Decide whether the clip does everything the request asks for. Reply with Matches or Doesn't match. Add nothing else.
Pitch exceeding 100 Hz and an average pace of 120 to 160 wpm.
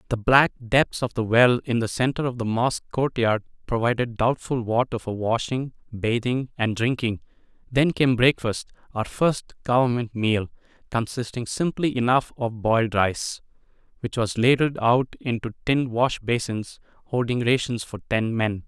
Matches